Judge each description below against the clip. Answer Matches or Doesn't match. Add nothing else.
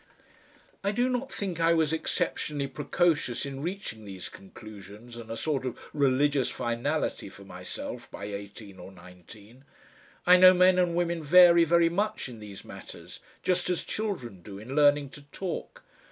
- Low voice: Doesn't match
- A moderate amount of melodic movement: Doesn't match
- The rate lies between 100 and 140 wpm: Doesn't match